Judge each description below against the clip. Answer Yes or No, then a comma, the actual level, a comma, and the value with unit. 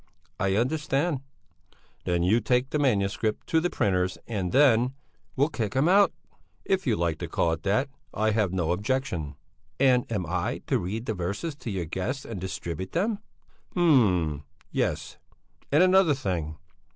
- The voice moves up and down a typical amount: No, wide, 7.0 semitones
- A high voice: No, low, 110 Hz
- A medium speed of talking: Yes, average, 160 wpm